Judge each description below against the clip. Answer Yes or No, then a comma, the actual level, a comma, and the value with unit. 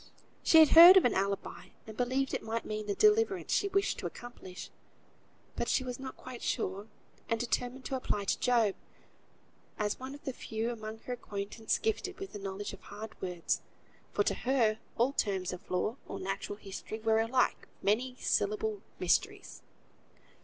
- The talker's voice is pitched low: No, high, 225 Hz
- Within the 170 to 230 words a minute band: Yes, average, 175 wpm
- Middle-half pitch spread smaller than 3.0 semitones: No, average, 4.1 semitones